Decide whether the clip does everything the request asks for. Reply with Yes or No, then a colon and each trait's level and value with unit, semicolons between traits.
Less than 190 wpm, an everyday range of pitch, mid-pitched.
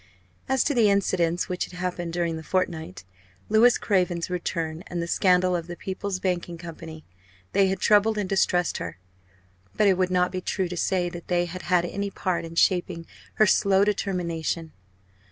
No: average, 180 wpm; narrow, 2.1 semitones; medium, 180 Hz